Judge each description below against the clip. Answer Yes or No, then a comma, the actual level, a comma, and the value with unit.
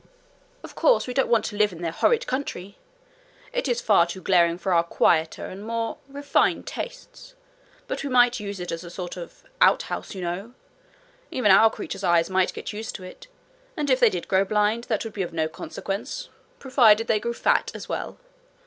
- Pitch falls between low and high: No, high, 210 Hz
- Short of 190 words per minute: No, average, 200 wpm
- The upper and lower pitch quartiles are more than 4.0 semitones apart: Yes, average, 5.1 semitones